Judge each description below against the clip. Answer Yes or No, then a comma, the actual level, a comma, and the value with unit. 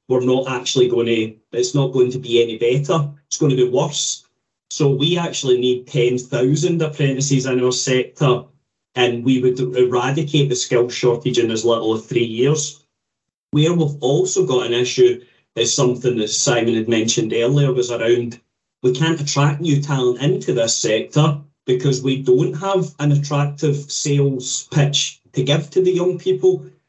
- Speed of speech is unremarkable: Yes, average, 170 wpm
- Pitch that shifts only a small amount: No, average, 3.1 semitones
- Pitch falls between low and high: No, low, 130 Hz